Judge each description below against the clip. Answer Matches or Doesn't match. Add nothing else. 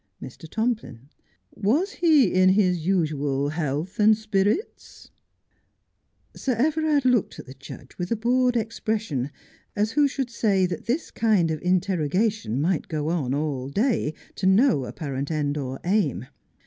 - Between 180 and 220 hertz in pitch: Matches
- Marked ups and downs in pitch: Matches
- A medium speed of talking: Matches